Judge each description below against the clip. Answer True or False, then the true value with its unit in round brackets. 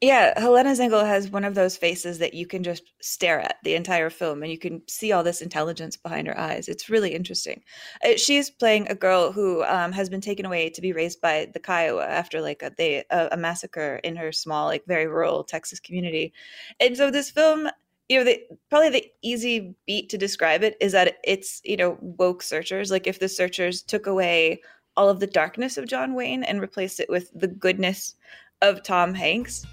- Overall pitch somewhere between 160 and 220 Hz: True (185 Hz)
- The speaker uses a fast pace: True (210 wpm)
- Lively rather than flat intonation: False (3.8 semitones)